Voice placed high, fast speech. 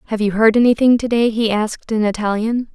Yes: high, 220 Hz; fast, 220 wpm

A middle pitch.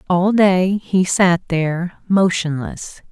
Yes: medium, 180 Hz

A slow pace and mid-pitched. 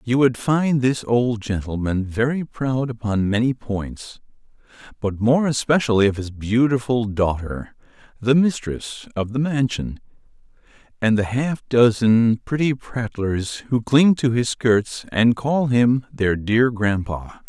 No: slow, 130 wpm; low, 120 Hz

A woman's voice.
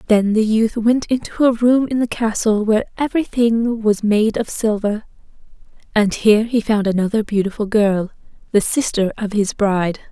Yes: female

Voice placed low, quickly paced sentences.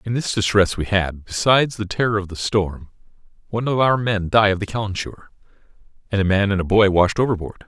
Yes: low, 100 Hz; fast, 210 wpm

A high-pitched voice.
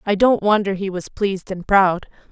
Yes: high, 195 Hz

